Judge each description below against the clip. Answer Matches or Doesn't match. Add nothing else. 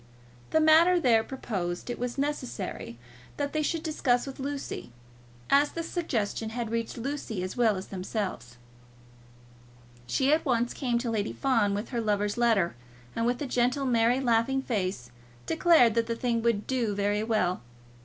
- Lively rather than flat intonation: Doesn't match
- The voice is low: Doesn't match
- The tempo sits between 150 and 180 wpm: Matches